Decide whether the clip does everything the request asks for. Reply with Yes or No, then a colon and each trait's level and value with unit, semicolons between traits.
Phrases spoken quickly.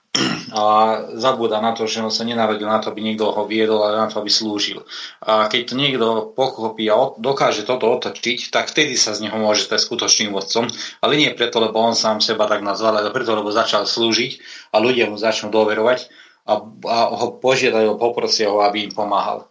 Yes: fast, 195 wpm